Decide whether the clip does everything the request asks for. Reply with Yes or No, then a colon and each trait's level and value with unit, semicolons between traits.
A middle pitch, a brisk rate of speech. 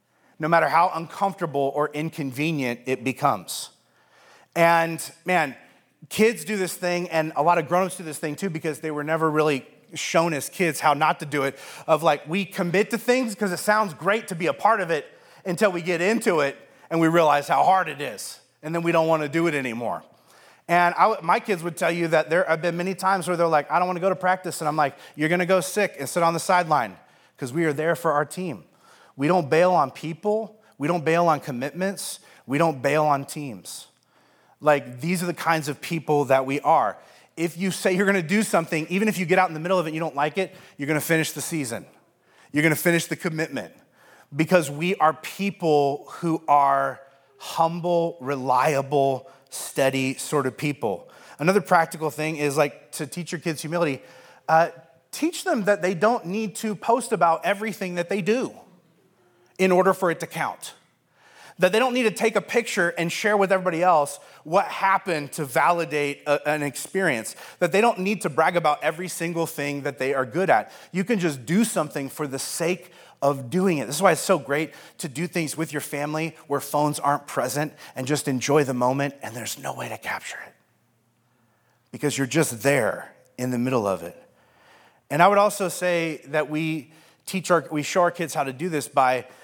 Yes: medium, 165 Hz; fast, 210 wpm